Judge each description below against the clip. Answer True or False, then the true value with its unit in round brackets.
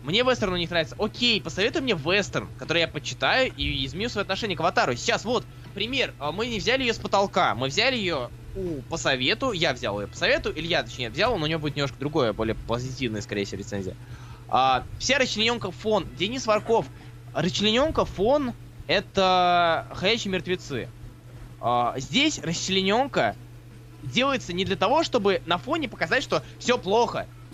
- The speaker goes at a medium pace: False (165 wpm)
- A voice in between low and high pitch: True (170 Hz)